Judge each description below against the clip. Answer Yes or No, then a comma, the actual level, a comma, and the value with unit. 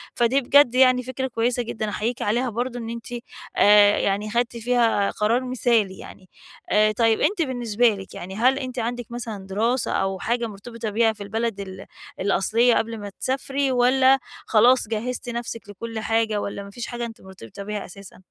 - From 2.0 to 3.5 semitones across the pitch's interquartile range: Yes, average, 2.9 semitones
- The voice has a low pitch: No, high, 230 Hz